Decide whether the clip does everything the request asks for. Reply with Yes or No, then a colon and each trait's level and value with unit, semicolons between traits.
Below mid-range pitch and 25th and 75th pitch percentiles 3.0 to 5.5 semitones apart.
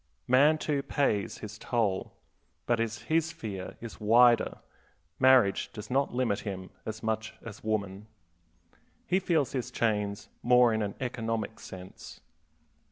Yes: low, 110 Hz; average, 3.6 semitones